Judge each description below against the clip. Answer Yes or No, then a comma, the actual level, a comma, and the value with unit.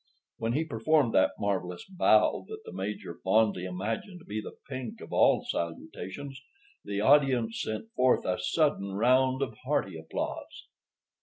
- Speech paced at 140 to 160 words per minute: Yes, average, 150 wpm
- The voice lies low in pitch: Yes, low, 115 Hz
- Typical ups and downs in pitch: No, wide, 5.8 semitones